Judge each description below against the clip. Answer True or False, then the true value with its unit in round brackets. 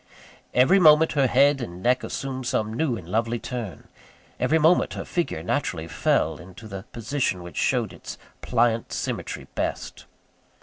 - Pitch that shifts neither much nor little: False (6.3 semitones)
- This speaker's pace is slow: False (155 wpm)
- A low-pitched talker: True (120 Hz)